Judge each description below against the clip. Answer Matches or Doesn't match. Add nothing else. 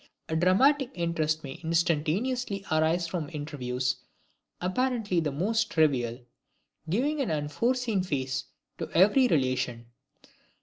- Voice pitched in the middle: Matches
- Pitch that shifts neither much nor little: Doesn't match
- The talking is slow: Matches